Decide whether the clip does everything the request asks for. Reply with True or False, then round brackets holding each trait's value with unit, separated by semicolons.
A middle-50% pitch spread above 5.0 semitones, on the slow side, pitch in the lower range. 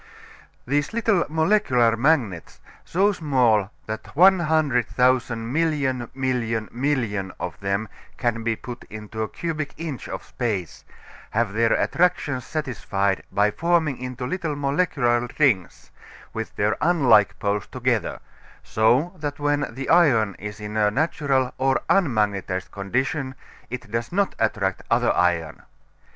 True (5.6 semitones; 125 wpm; 125 Hz)